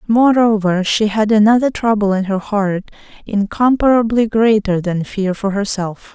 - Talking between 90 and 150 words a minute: Yes, slow, 135 wpm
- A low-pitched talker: No, high, 210 Hz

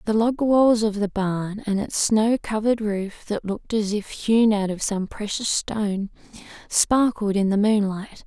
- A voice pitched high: Yes, high, 210 Hz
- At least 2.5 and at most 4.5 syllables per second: Yes, 4.3 syllables/s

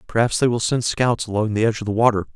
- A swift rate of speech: Yes, fast, 280 wpm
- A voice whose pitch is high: No, low, 115 Hz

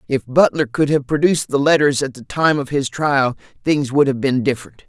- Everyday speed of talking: No, fast, 220 wpm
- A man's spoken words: Yes, male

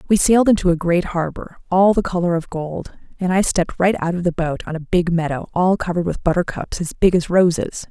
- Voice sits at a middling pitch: Yes, medium, 175 Hz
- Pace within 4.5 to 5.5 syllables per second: No, 5.8 syllables/s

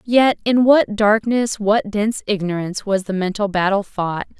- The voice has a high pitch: Yes, high, 205 Hz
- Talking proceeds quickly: No, average, 165 wpm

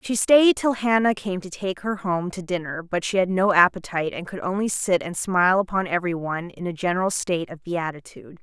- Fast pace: Yes, fast, 215 wpm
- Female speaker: Yes, female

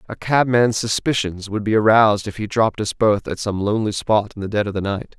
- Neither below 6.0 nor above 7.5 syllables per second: No, 5.8 syllables/s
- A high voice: No, low, 105 Hz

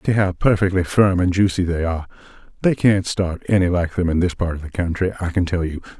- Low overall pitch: Yes, very low, 90 Hz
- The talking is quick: Yes, fast, 230 wpm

